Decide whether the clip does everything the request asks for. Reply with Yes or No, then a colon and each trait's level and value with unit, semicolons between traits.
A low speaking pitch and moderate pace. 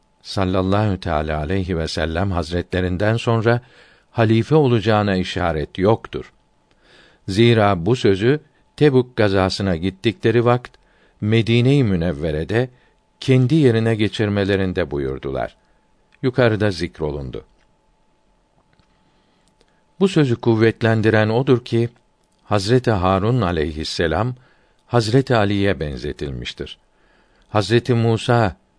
No: low, 105 Hz; slow, 80 wpm